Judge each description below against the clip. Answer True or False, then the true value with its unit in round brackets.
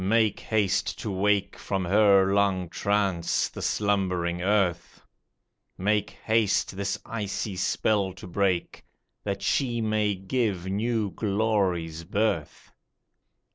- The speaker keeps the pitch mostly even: True (2.2 semitones)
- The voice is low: True (100 Hz)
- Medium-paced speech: False (110 wpm)